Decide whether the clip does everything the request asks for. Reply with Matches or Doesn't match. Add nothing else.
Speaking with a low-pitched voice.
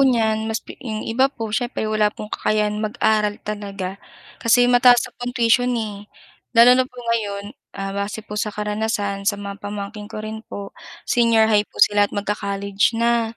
Doesn't match